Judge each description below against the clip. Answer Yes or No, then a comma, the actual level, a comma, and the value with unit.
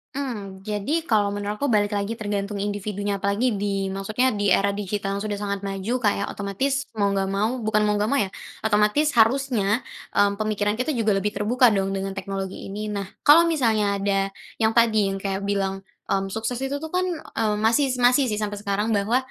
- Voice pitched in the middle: No, high, 210 Hz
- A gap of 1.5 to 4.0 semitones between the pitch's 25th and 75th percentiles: Yes, average, 2.7 semitones